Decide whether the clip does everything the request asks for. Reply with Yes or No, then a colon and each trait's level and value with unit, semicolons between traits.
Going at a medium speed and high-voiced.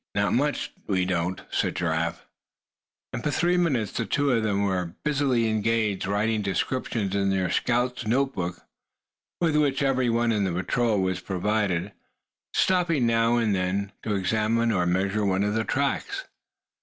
No: average, 160 wpm; low, 110 Hz